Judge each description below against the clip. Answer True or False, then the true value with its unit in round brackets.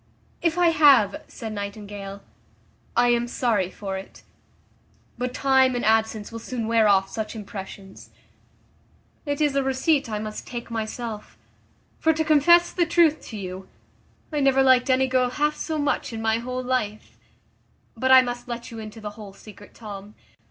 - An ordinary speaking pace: True (165 wpm)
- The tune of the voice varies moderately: True (4.0 semitones)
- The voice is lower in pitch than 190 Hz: False (235 Hz)